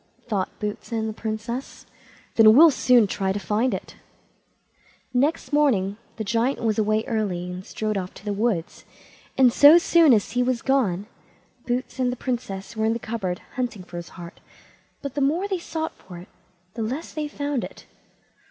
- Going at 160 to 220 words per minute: Yes, average, 180 wpm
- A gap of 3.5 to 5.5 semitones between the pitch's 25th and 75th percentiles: Yes, average, 4.4 semitones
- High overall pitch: Yes, high, 225 Hz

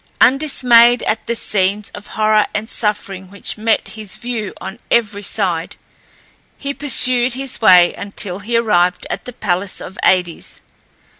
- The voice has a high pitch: Yes, high, 215 Hz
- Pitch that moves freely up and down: No, average, 3.8 semitones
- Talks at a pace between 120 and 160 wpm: Yes, average, 145 wpm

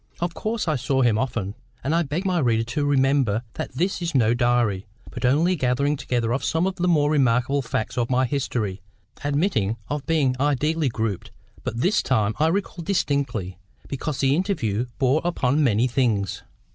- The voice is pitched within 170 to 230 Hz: No, low, 135 Hz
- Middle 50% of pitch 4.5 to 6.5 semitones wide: Yes, average, 4.9 semitones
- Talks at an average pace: Yes, average, 175 wpm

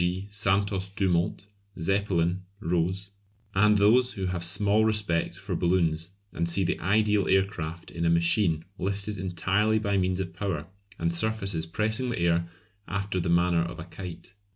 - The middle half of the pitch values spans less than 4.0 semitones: Yes, average, 3.1 semitones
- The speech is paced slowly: No, average, 160 wpm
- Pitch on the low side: Yes, very low, 95 Hz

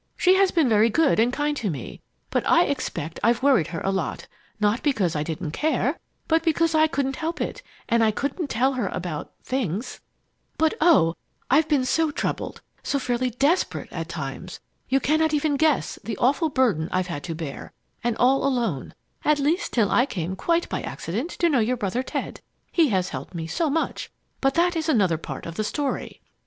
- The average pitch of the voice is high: Yes, very high, 255 Hz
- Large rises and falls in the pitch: Yes, wide, 7.9 semitones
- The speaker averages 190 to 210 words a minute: Yes, average, 200 wpm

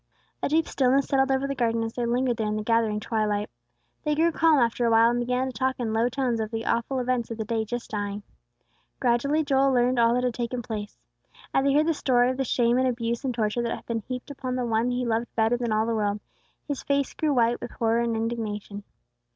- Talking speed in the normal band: No, fast, 240 wpm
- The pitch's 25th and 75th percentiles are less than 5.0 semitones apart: Yes, narrow, 2.4 semitones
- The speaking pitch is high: Yes, high, 240 Hz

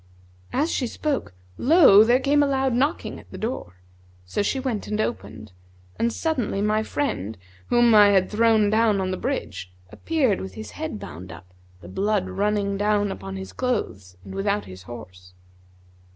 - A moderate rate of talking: Yes, average, 170 wpm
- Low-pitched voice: No, high, 210 Hz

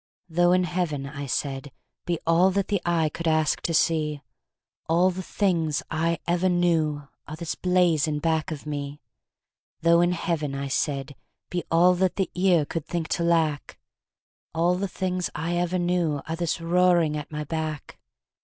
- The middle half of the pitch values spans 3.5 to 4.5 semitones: No, narrow, 2.6 semitones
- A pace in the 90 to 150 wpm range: No, average, 175 wpm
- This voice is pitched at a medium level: Yes, medium, 165 Hz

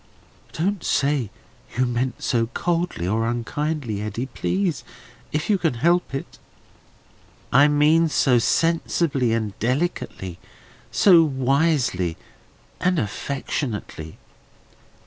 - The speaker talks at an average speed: No, slow, 100 wpm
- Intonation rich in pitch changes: Yes, wide, 6.1 semitones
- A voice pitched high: No, low, 135 Hz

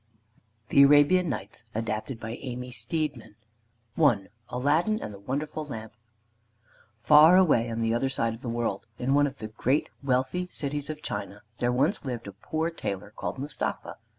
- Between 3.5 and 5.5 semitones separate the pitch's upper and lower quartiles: Yes, average, 4.7 semitones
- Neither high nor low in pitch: No, low, 130 Hz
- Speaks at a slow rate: No, average, 165 wpm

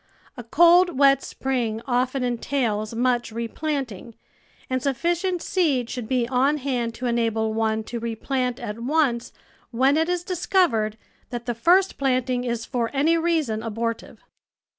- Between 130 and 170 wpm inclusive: Yes, average, 140 wpm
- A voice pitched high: Yes, very high, 250 Hz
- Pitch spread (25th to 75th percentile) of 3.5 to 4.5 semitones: Yes, average, 3.8 semitones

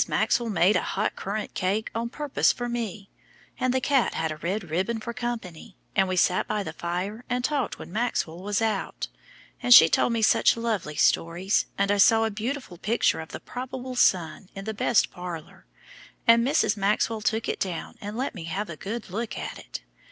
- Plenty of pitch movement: No, average, 4.3 semitones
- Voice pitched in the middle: No, high, 210 Hz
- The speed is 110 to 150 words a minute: No, average, 200 wpm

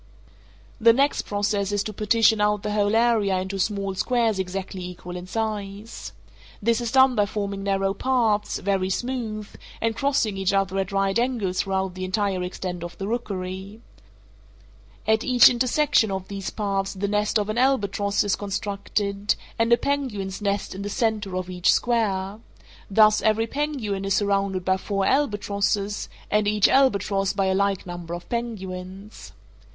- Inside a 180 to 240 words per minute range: No, average, 160 wpm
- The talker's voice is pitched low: No, high, 205 Hz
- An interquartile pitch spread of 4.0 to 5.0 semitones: No, narrow, 2.5 semitones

